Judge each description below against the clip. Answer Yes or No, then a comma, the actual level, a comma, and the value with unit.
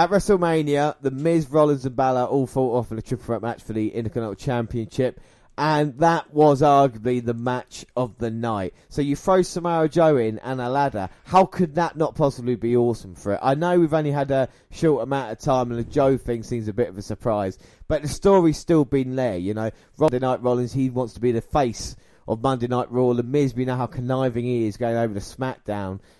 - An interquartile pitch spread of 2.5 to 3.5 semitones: No, average, 3.9 semitones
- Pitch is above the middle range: No, low, 125 Hz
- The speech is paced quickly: Yes, fast, 225 wpm